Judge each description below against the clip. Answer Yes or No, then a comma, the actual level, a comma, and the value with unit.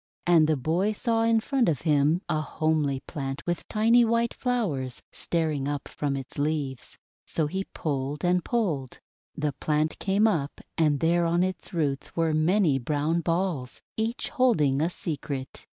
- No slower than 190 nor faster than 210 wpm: No, average, 160 wpm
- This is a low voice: No, medium, 160 Hz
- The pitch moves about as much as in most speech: Yes, average, 4.8 semitones